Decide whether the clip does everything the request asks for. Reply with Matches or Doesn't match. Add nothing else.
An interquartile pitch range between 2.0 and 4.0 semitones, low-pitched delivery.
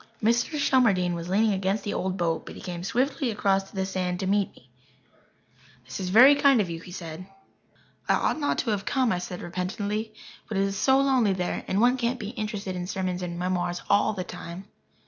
Doesn't match